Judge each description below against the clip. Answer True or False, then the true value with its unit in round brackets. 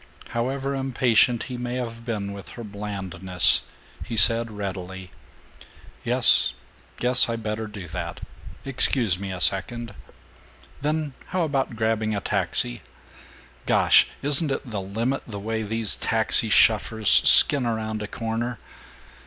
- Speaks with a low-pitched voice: True (110 Hz)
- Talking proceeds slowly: True (130 wpm)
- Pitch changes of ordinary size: True (3.3 semitones)